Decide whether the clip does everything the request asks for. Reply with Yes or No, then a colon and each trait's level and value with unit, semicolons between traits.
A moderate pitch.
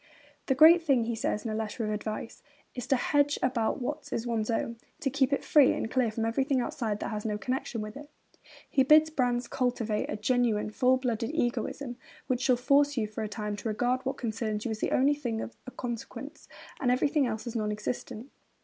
No: high, 245 Hz